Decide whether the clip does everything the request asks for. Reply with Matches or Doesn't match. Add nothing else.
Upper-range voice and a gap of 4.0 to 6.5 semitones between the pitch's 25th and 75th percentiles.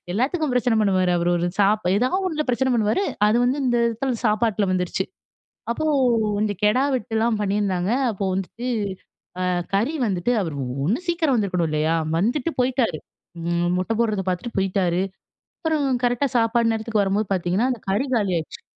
Matches